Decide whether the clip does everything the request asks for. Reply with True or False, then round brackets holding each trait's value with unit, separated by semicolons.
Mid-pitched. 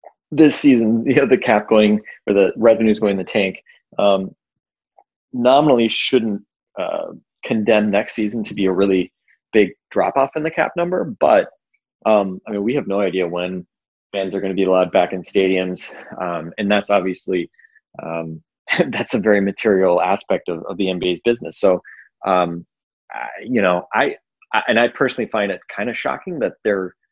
False (100 Hz)